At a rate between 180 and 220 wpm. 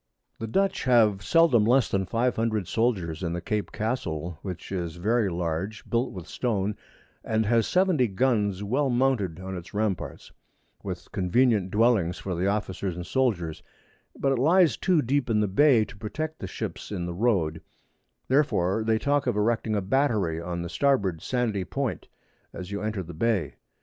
No: average, 170 wpm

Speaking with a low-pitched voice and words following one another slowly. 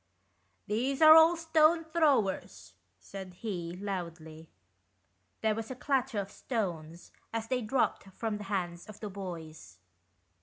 No: high, 210 Hz; slow, 130 wpm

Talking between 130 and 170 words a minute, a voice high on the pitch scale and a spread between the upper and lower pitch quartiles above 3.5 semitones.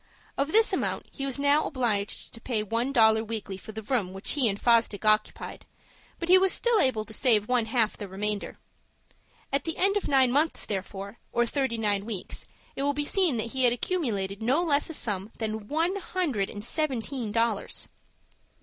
No: average, 195 wpm; high, 235 Hz; average, 5.0 semitones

